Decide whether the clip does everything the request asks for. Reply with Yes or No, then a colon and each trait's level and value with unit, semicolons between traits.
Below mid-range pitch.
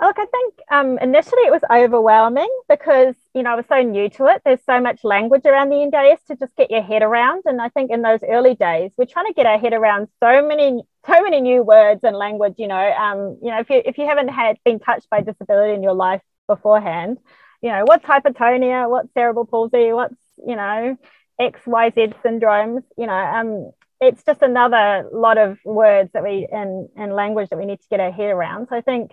No: high, 240 Hz